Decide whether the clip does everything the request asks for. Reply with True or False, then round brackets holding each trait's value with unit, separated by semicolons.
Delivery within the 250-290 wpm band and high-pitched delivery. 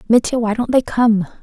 False (210 wpm; 225 Hz)